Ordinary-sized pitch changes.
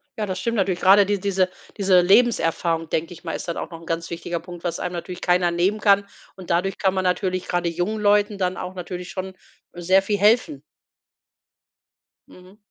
No: narrow, 2.2 semitones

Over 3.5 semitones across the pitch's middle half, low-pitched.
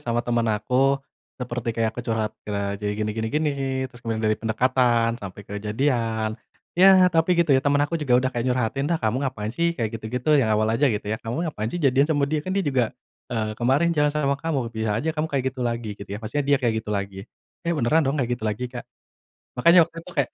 Yes: average, 4.4 semitones; low, 125 Hz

